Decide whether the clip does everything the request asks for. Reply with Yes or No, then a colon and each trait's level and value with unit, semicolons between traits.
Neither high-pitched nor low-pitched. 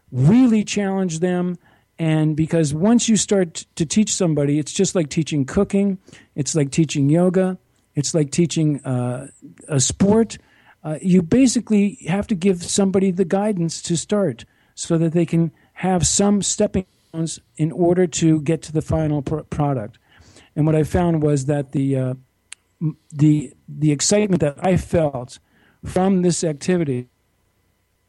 Yes: medium, 165 Hz